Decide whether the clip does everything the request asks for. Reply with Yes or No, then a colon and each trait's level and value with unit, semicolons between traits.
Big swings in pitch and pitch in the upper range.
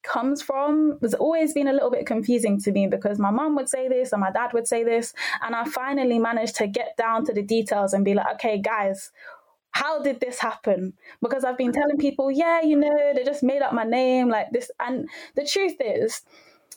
No: average, 4.2 semitones; very high, 255 Hz